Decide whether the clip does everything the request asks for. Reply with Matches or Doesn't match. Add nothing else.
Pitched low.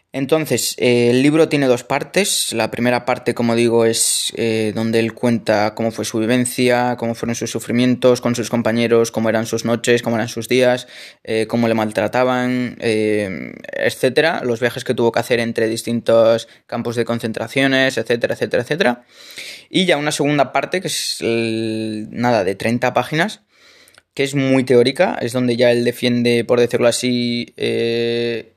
Matches